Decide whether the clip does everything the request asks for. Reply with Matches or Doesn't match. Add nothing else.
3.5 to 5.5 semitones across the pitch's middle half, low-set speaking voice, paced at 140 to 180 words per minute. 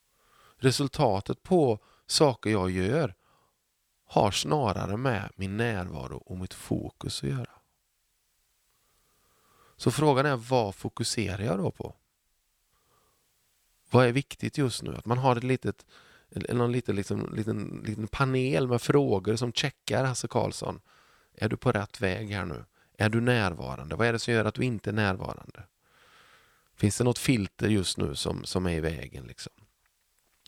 Matches